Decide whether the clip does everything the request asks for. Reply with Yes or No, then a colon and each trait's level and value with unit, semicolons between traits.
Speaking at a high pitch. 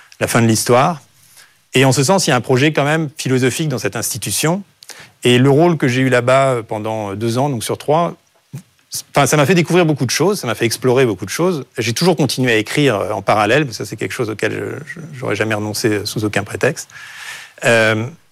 No: low, 130 Hz